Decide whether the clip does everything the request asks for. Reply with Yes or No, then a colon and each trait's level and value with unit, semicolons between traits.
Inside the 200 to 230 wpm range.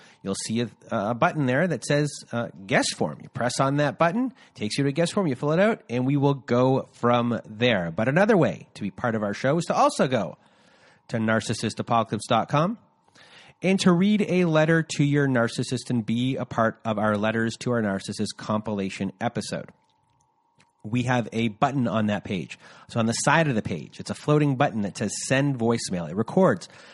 Yes: fast, 205 wpm